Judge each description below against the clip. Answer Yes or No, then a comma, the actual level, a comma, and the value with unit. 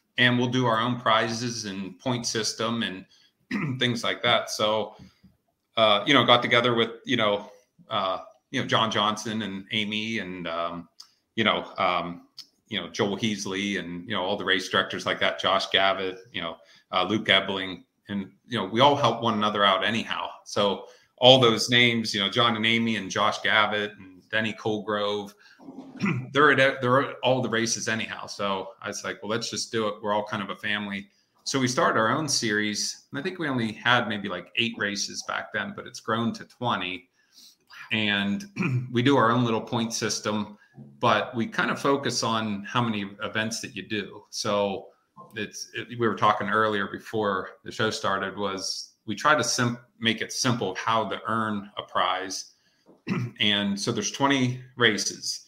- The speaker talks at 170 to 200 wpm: Yes, average, 190 wpm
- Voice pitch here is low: Yes, low, 110 Hz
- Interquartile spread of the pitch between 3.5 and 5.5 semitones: No, average, 3.1 semitones